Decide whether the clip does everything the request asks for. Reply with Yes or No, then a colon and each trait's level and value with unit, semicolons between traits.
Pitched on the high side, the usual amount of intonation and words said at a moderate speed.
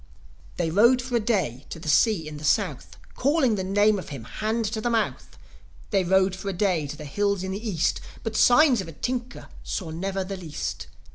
No: high, 195 Hz; average, 4.8 semitones; fast, 215 wpm